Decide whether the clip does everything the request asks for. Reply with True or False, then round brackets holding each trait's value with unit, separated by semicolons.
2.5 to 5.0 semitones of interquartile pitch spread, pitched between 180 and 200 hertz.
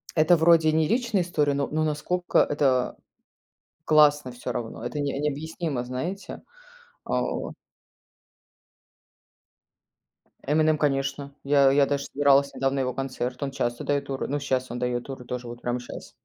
False (3.0 semitones; 140 Hz)